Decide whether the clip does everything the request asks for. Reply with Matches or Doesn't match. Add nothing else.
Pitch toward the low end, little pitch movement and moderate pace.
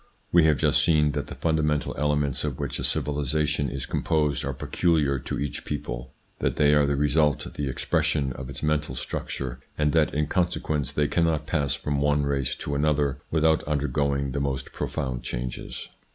Matches